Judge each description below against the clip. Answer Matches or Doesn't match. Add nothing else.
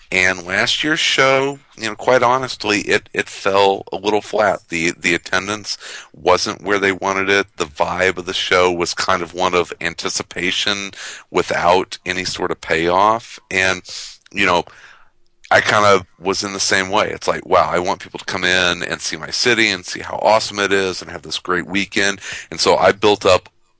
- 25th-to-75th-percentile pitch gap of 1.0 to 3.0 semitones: Matches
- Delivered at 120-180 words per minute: Doesn't match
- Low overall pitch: Matches